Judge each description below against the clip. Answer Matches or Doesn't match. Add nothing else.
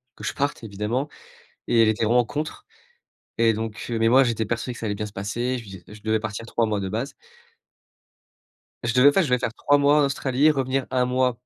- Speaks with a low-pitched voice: Matches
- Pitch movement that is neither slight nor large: Matches